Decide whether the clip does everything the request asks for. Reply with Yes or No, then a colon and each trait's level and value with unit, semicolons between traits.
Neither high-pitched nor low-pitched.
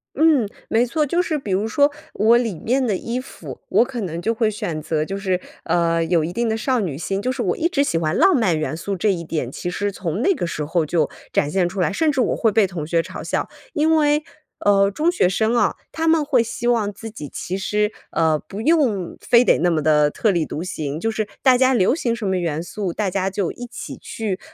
No: high, 205 Hz